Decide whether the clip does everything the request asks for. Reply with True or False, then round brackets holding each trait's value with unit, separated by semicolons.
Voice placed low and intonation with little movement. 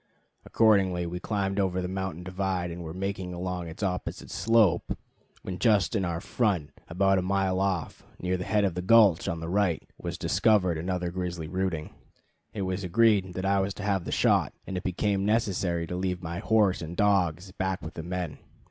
True (95 Hz; 2.0 semitones)